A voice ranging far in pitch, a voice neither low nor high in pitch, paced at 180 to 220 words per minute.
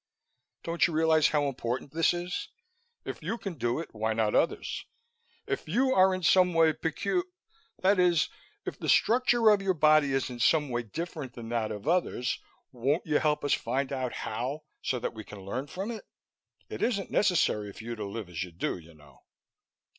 Yes: wide, 7.2 semitones; medium, 150 Hz; average, 195 wpm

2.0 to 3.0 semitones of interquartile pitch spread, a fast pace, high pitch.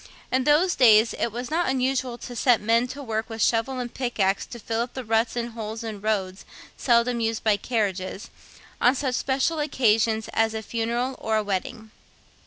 No: narrow, 2.5 semitones; average, 185 wpm; high, 230 Hz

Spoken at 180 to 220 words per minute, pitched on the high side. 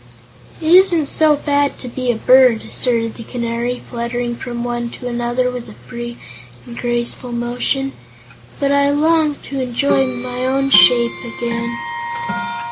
No: average, 145 wpm; high, 245 Hz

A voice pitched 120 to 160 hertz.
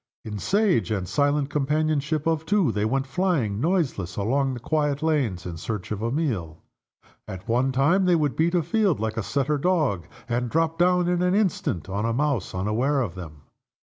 Yes: medium, 140 Hz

